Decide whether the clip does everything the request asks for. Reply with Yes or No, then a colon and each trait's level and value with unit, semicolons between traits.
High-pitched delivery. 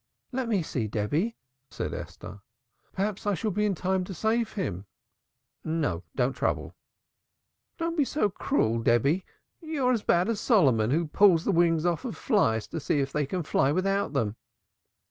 No: medium, 180 Hz